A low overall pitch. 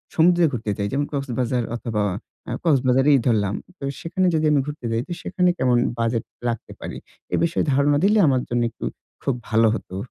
Yes: low, 130 Hz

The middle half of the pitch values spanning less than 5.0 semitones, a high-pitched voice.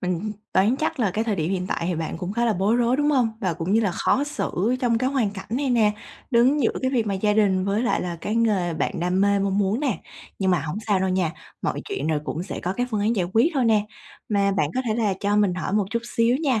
Yes: average, 4.0 semitones; high, 210 Hz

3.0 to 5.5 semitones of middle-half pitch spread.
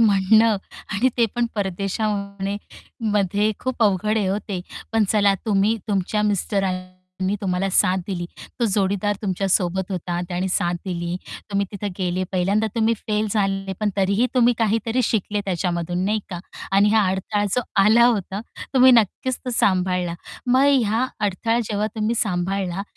No: narrow, 2.5 semitones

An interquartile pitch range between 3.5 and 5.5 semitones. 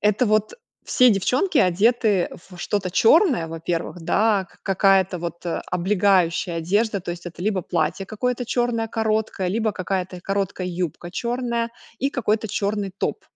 Yes: average, 3.8 semitones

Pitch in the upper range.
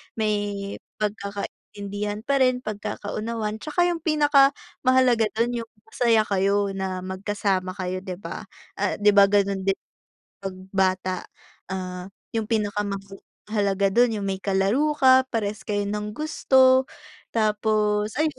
Yes: high, 210 Hz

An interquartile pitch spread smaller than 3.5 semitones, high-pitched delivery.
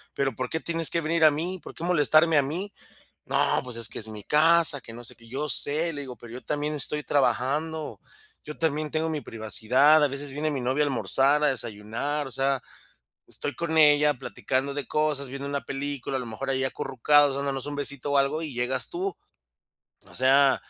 No: narrow, 2.6 semitones; medium, 140 Hz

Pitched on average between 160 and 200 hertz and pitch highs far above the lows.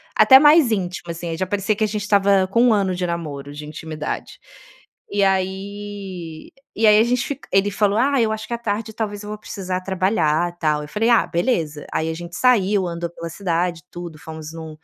No: high, 190 Hz; average, 4.0 semitones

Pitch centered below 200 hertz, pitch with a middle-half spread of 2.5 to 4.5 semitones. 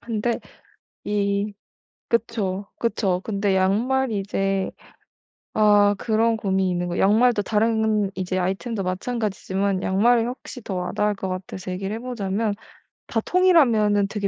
No: high, 205 Hz; average, 3.0 semitones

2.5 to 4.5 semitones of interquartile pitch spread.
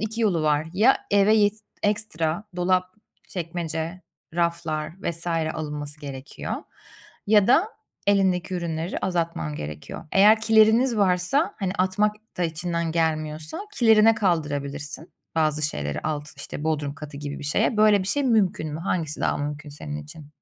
No: average, 5.0 semitones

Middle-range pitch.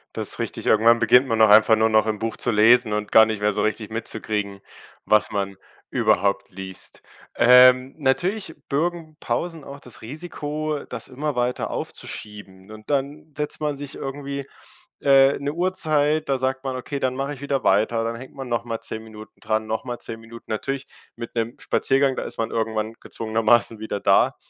No: low, 120 Hz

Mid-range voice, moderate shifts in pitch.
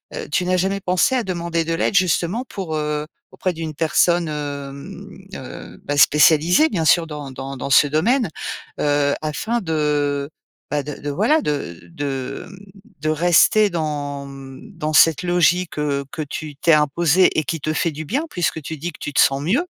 Yes: medium, 155 Hz; average, 3.4 semitones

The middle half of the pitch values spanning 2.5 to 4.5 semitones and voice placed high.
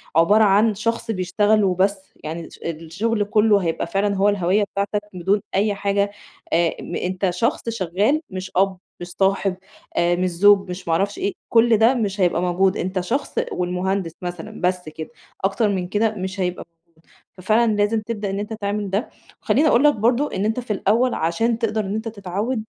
Yes: average, 3.1 semitones; high, 200 Hz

